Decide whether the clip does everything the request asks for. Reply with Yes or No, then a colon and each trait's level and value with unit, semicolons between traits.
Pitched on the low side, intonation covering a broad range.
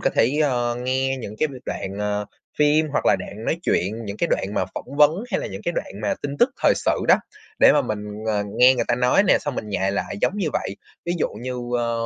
Yes: low, 125 Hz; wide, 5.9 semitones